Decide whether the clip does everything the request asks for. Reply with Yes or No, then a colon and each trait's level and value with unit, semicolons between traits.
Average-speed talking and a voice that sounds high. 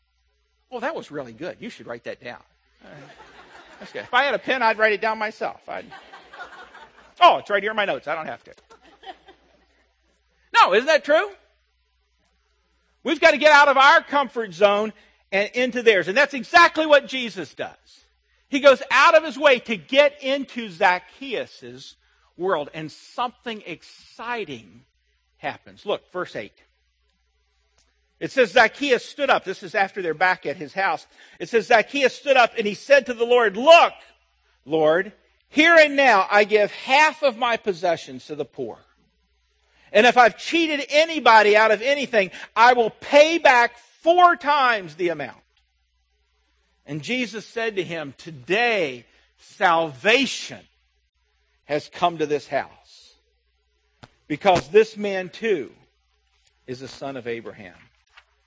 Yes: average, 155 wpm; high, 210 Hz